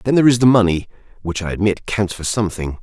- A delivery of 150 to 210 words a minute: No, fast, 235 wpm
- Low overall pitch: Yes, low, 100 Hz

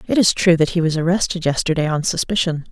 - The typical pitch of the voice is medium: Yes, medium, 170 Hz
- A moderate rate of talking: No, fast, 220 wpm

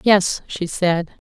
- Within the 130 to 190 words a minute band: Yes, average, 140 wpm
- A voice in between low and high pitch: Yes, medium, 180 Hz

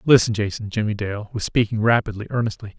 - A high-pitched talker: No, low, 110 Hz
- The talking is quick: No, average, 175 wpm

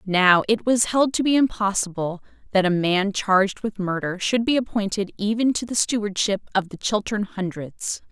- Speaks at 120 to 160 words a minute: No, average, 180 wpm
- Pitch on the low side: No, high, 205 Hz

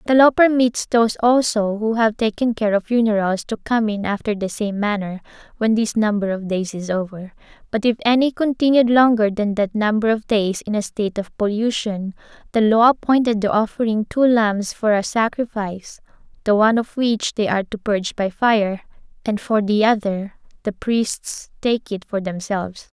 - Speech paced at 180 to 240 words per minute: Yes, average, 185 wpm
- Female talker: Yes, female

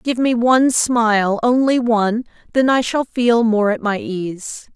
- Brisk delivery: No, average, 150 wpm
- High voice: Yes, high, 230 Hz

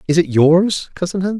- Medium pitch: Yes, medium, 175 Hz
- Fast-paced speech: Yes, fast, 215 wpm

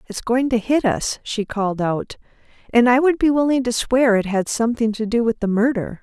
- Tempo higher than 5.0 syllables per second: Yes, 5.3 syllables/s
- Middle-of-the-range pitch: No, high, 235 Hz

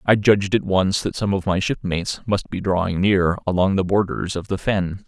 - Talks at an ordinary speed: No, fast, 225 wpm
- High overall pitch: No, very low, 95 Hz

